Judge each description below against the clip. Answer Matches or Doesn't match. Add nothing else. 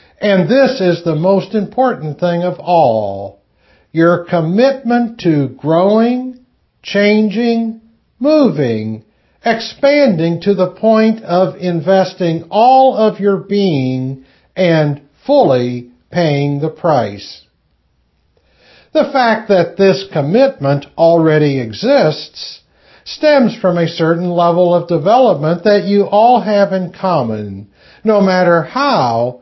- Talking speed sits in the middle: Doesn't match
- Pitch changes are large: Matches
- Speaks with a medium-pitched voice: Matches